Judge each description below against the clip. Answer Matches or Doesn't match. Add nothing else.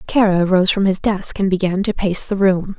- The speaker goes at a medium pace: Doesn't match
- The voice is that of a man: Doesn't match